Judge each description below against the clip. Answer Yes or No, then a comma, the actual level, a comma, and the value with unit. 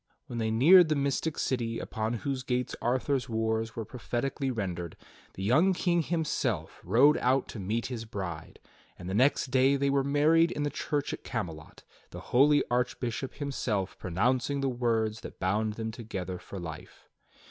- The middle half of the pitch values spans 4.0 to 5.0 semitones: Yes, average, 4.3 semitones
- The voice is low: Yes, low, 120 Hz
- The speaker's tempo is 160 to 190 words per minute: Yes, average, 170 wpm